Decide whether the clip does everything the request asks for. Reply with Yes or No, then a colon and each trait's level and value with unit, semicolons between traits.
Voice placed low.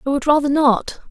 No: very high, 280 Hz